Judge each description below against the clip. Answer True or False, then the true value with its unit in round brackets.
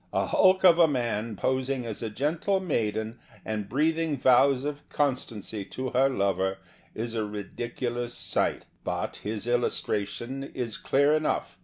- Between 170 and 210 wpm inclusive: False (150 wpm)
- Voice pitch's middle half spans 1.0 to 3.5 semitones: False (4.5 semitones)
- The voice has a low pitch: True (120 Hz)